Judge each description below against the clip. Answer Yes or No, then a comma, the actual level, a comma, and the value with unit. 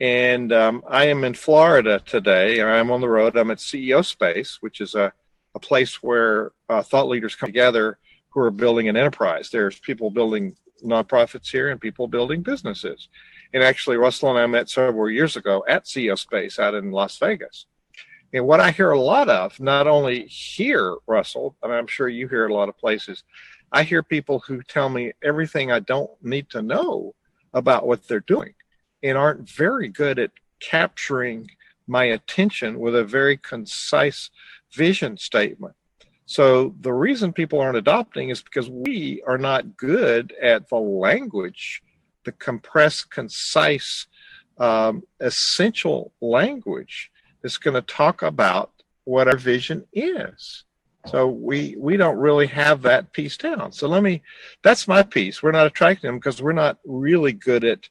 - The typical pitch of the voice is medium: No, low, 130 Hz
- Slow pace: No, average, 170 wpm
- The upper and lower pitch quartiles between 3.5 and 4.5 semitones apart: Yes, average, 4.0 semitones